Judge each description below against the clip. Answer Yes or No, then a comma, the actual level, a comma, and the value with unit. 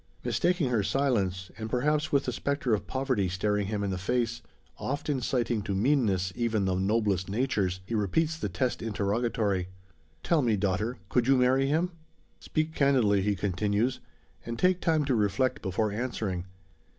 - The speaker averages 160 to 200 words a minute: Yes, average, 165 wpm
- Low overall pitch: Yes, low, 115 Hz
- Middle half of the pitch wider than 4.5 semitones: Yes, average, 5.1 semitones